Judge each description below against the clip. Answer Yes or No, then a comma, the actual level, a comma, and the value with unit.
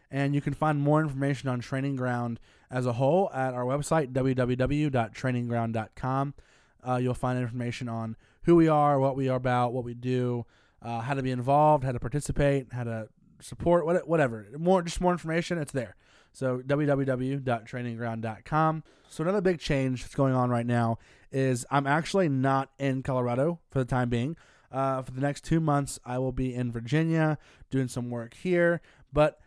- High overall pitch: No, low, 135 Hz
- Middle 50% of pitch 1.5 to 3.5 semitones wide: Yes, average, 3.0 semitones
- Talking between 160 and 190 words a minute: Yes, average, 175 wpm